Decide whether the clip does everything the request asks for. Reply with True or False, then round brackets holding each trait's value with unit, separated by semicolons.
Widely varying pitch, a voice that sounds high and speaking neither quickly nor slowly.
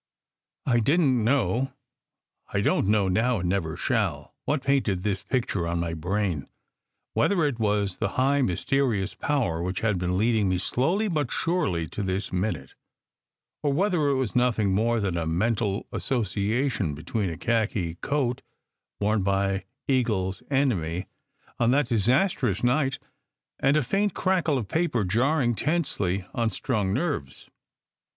False (6.1 semitones; 110 Hz; 155 wpm)